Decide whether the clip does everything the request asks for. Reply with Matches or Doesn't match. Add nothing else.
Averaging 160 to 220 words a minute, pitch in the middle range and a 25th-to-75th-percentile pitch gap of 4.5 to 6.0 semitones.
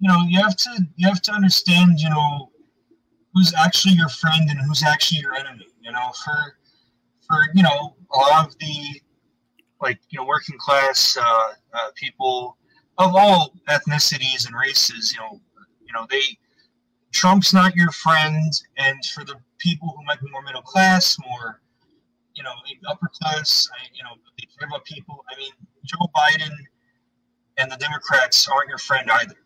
Matches